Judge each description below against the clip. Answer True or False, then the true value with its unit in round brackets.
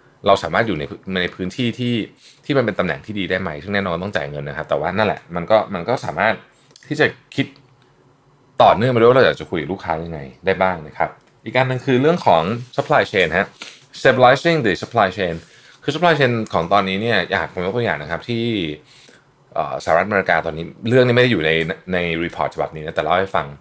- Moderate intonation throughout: False (6.5 semitones)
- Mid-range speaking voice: False (105 Hz)